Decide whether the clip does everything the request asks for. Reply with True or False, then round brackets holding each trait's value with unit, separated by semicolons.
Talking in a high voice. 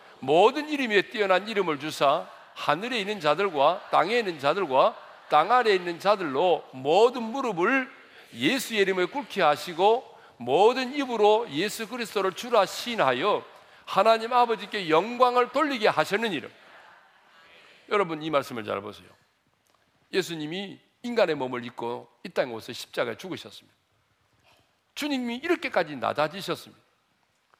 True (210 Hz)